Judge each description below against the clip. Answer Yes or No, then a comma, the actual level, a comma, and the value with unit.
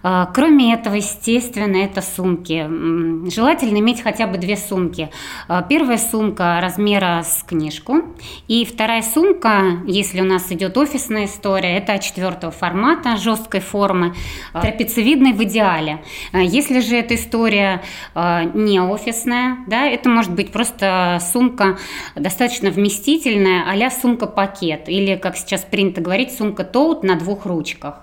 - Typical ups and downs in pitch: Yes, average, 4.3 semitones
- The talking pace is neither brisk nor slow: Yes, average, 125 wpm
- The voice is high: Yes, high, 200 Hz